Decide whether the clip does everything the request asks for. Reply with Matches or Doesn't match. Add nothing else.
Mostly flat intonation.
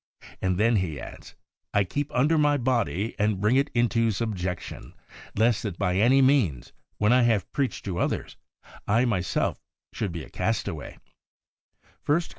Doesn't match